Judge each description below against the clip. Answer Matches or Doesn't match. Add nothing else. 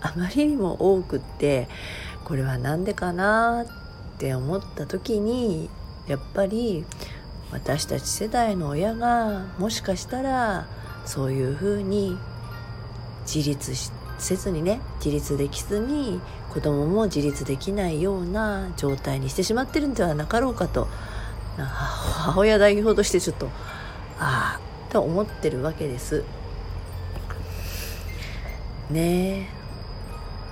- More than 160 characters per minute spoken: Matches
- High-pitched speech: Doesn't match